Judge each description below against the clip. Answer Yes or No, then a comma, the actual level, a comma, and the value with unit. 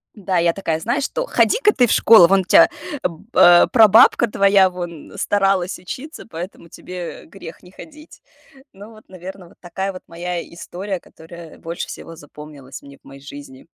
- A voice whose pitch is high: No, medium, 180 Hz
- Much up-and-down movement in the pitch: No, average, 3.0 semitones